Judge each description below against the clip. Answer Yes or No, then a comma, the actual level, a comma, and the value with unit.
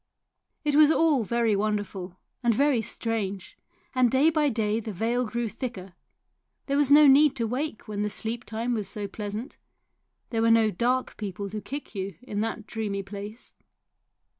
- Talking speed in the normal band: Yes, average, 165 wpm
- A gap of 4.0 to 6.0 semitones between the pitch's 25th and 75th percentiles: No, average, 3.6 semitones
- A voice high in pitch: Yes, high, 225 Hz